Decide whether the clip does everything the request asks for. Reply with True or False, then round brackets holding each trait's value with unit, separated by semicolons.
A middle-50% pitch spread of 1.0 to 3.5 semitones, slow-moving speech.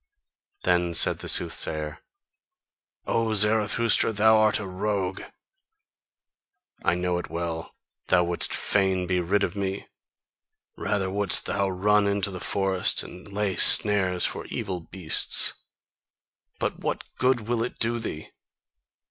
True (2.7 semitones; 130 wpm)